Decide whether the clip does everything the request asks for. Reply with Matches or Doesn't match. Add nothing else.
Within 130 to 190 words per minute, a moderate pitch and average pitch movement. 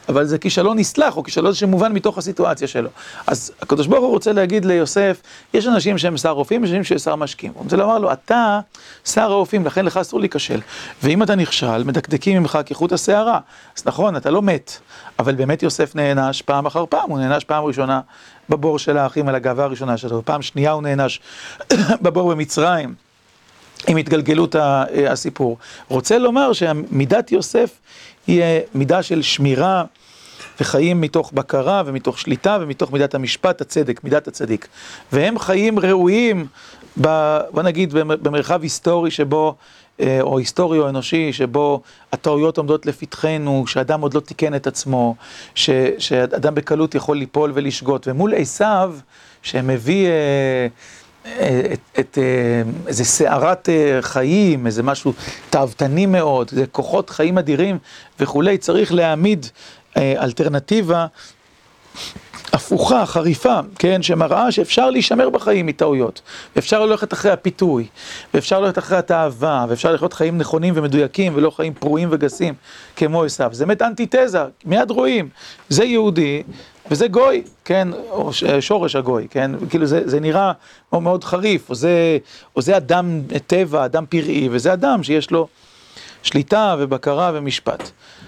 Matches